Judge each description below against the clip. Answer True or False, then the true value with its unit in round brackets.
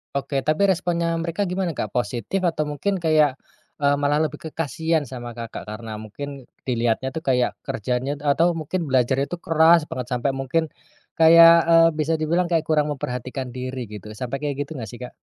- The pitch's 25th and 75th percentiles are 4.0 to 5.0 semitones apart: True (4.5 semitones)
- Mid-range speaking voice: True (145 Hz)